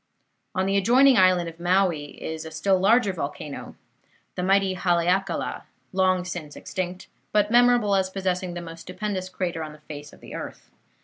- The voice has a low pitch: No, medium, 185 Hz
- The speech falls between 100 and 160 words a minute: No, average, 170 wpm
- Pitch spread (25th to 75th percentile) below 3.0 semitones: Yes, narrow, 2.4 semitones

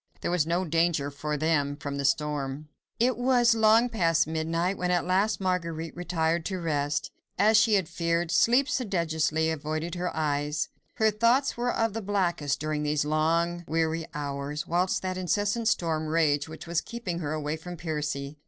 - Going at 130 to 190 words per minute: Yes, average, 170 wpm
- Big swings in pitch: No, average, 3.7 semitones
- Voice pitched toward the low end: No, medium, 165 Hz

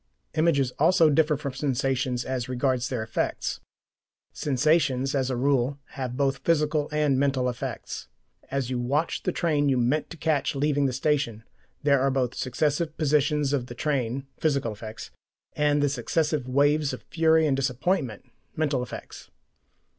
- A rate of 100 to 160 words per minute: Yes, average, 155 wpm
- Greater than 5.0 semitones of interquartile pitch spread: No, average, 2.8 semitones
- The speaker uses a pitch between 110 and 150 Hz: Yes, medium, 140 Hz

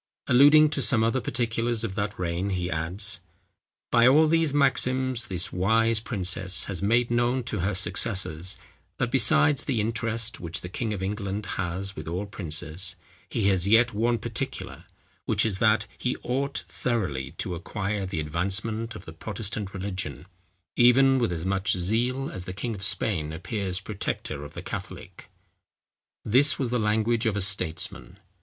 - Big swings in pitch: No, average, 4.3 semitones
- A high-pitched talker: No, low, 105 Hz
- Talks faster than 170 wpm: No, average, 160 wpm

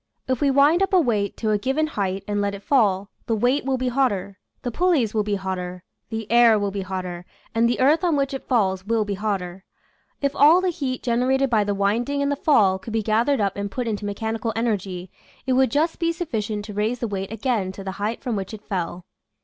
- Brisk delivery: Yes, fast, 235 wpm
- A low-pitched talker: No, high, 220 Hz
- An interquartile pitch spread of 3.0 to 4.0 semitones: No, average, 4.8 semitones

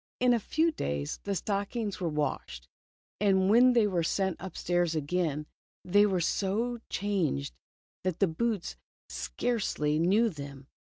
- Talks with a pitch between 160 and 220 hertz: Yes, high, 190 Hz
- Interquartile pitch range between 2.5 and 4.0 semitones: No, average, 4.7 semitones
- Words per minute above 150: No, slow, 135 wpm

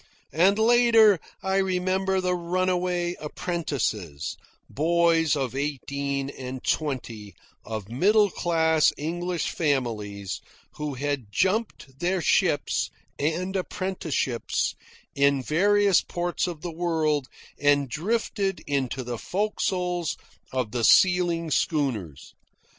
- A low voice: No, medium, 160 Hz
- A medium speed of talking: No, slow, 105 wpm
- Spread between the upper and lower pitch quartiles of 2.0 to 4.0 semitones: No, average, 5.2 semitones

